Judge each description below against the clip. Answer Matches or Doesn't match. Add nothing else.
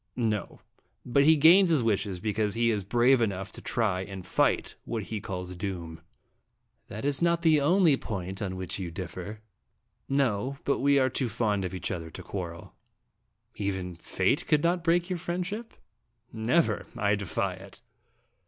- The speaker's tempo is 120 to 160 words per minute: Doesn't match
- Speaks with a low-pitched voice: Matches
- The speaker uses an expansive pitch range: Matches